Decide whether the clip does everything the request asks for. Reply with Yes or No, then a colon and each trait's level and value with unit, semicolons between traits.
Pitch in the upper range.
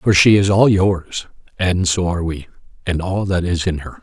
No: very low, 90 Hz